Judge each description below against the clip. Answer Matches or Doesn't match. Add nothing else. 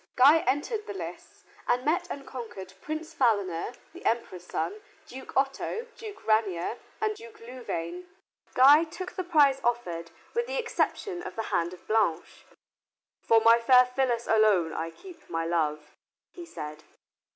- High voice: Matches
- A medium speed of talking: Matches